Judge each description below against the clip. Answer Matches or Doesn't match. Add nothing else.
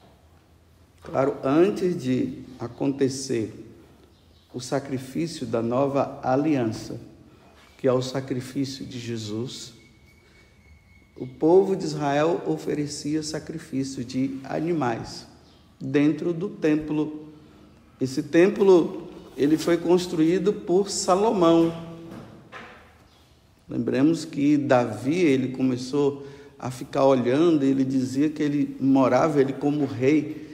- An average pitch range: Matches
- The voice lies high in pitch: Doesn't match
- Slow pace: Matches